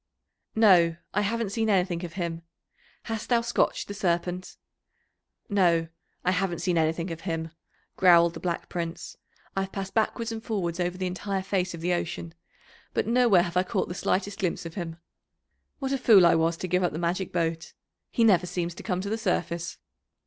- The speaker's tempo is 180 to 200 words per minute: Yes, average, 190 wpm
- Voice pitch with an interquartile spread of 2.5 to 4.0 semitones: Yes, average, 2.9 semitones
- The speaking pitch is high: No, medium, 180 Hz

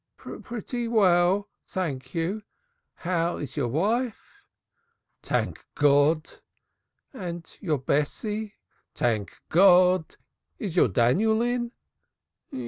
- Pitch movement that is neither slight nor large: No, wide, 6.4 semitones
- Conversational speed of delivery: No, slow, 90 wpm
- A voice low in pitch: No, medium, 180 Hz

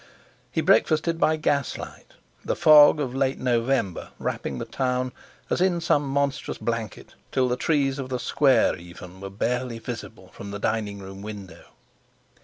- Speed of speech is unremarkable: Yes, average, 155 wpm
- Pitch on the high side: No, low, 125 Hz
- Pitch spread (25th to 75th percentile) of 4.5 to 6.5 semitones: Yes, average, 5.2 semitones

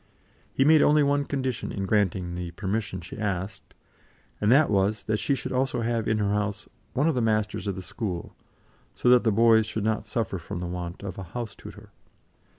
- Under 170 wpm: No, fast, 205 wpm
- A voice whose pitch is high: No, low, 105 Hz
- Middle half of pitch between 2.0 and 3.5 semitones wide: No, average, 3.9 semitones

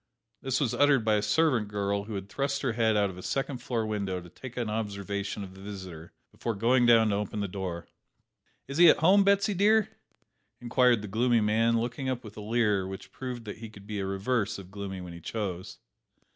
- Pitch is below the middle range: Yes, low, 110 Hz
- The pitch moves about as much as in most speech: Yes, average, 3.8 semitones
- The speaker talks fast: Yes, fast, 220 wpm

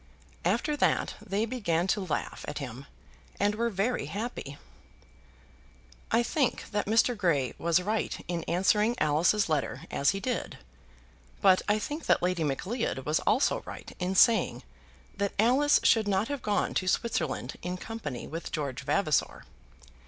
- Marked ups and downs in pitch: Yes, wide, 5.7 semitones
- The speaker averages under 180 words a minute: Yes, average, 150 wpm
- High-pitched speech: Yes, high, 195 Hz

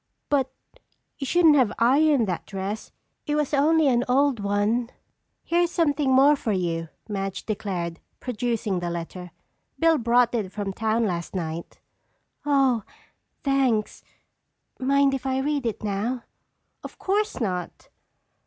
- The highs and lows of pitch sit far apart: Yes, wide, 5.8 semitones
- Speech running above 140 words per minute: No, slow, 135 wpm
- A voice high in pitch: Yes, high, 240 Hz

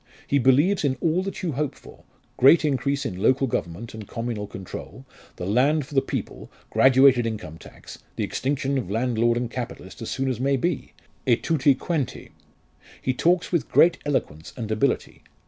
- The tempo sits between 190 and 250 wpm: No, average, 175 wpm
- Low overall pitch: Yes, low, 130 Hz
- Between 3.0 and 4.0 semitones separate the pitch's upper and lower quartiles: Yes, average, 3.7 semitones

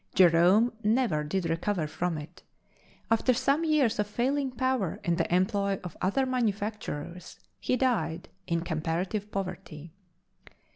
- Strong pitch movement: Yes, wide, 6.2 semitones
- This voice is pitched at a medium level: No, high, 195 Hz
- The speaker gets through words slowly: Yes, slow, 130 wpm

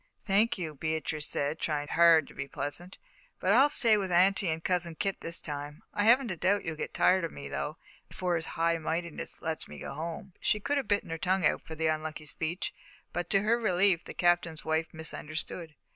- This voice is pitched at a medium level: Yes, medium, 170 Hz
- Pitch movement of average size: Yes, average, 3.2 semitones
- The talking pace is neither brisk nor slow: No, fast, 210 wpm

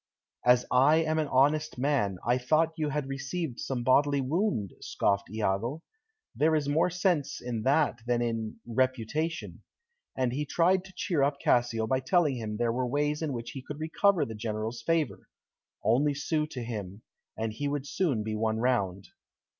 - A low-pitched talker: Yes, low, 130 Hz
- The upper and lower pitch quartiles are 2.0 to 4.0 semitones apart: No, average, 4.9 semitones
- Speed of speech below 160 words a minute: No, average, 175 wpm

